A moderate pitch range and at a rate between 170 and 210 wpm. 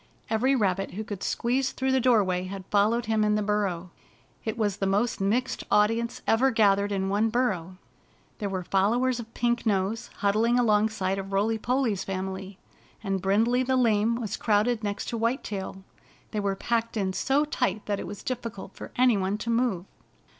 Yes: average, 3.3 semitones; average, 180 wpm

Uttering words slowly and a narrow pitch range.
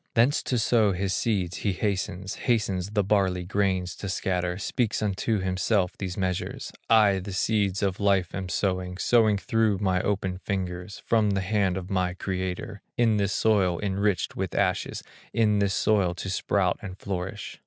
No: average, 165 wpm; narrow, 2.2 semitones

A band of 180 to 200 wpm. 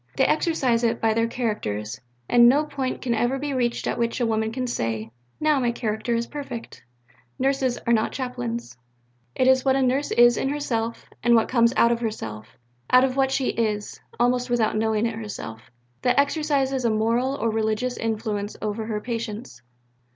Yes: average, 185 wpm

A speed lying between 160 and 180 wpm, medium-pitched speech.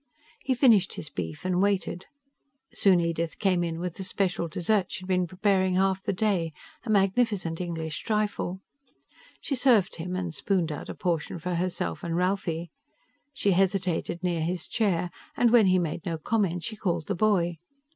Yes: average, 170 wpm; medium, 180 Hz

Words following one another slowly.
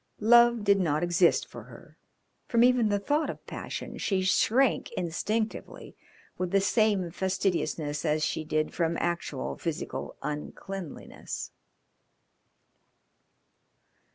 Yes: slow, 110 wpm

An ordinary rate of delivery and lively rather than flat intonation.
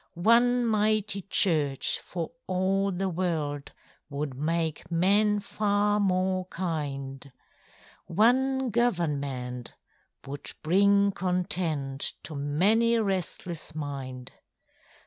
No: slow, 90 wpm; wide, 5.7 semitones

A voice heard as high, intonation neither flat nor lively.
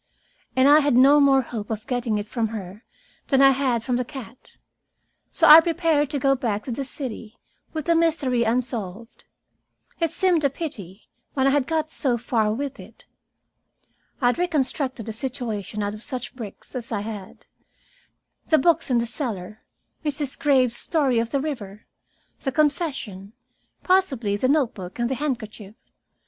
Yes: very high, 255 Hz; average, 4.5 semitones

